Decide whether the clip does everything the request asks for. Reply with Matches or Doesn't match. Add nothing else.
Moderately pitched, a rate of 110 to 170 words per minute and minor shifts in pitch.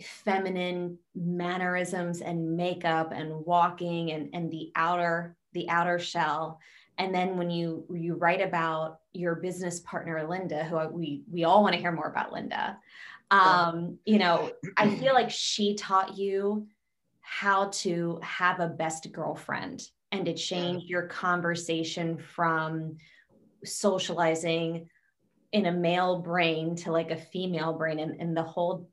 Matches